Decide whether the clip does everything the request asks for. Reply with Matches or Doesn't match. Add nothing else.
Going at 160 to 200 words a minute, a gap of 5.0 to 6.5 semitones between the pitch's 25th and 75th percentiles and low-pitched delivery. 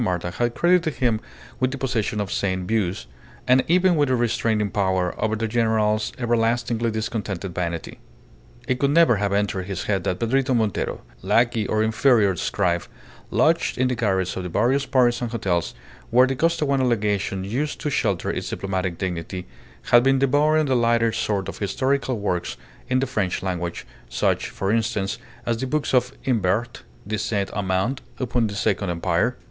Doesn't match